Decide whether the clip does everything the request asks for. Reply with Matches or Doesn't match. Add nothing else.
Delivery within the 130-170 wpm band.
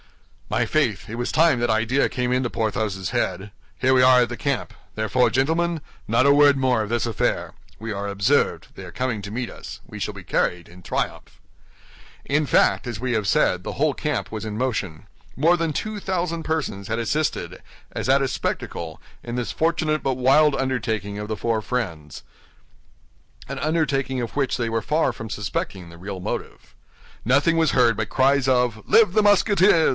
Doesn't match